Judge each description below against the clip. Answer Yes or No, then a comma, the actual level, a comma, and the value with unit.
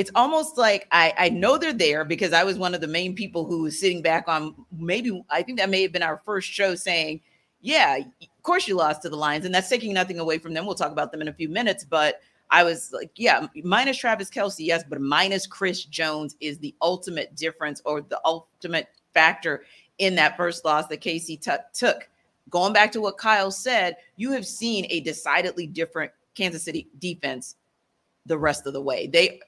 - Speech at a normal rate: No, fast, 215 wpm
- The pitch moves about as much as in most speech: Yes, average, 3.7 semitones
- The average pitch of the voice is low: No, medium, 175 Hz